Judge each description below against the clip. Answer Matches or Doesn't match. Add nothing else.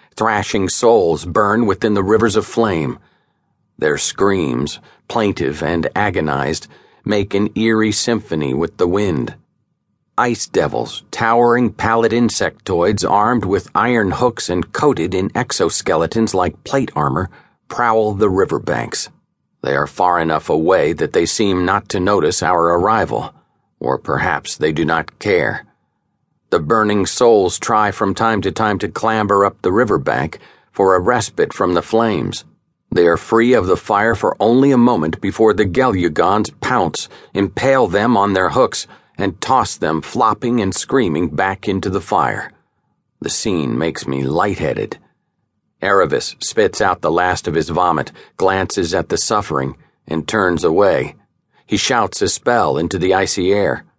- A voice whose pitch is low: Matches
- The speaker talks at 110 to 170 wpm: Matches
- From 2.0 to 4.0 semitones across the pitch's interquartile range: Matches